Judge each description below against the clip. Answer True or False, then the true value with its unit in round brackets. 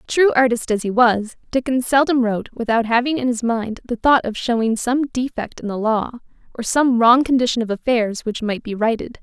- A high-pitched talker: True (235 Hz)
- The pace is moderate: False (210 wpm)